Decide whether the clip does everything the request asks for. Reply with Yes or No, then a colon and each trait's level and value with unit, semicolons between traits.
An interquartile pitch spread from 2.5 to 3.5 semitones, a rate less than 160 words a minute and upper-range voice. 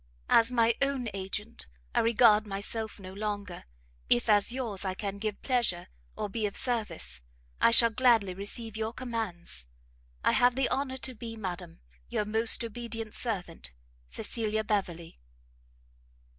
Yes: average, 3.0 semitones; average, 145 wpm; high, 215 Hz